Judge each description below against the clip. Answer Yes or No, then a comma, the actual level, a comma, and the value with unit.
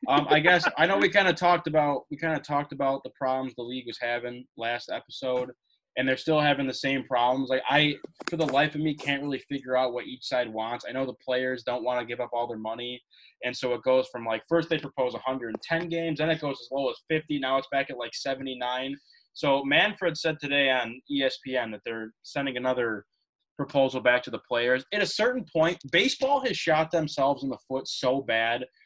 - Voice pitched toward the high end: No, low, 135 Hz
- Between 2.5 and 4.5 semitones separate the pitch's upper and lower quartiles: Yes, average, 3.6 semitones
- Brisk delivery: Yes, fast, 225 wpm